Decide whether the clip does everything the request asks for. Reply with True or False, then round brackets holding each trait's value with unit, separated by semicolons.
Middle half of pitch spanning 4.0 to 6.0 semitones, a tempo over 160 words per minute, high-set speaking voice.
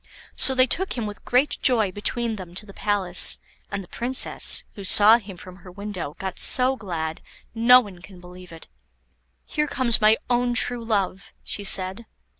True (4.5 semitones; 180 wpm; 205 Hz)